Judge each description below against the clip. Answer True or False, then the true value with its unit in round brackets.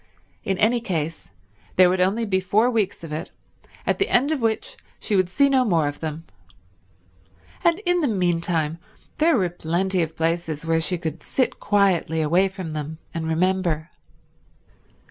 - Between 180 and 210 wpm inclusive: False (165 wpm)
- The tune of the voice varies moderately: True (4.6 semitones)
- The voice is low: False (180 Hz)